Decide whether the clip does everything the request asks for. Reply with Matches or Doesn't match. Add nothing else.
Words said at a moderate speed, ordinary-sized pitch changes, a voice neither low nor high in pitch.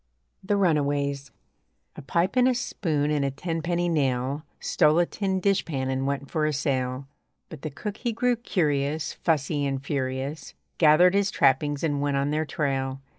Matches